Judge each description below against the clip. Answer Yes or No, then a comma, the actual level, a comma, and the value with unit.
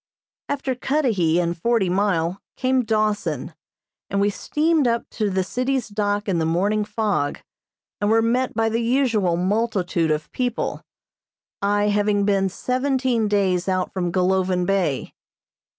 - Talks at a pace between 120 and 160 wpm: Yes, average, 140 wpm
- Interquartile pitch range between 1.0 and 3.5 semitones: No, average, 4.2 semitones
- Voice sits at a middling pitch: No, high, 205 Hz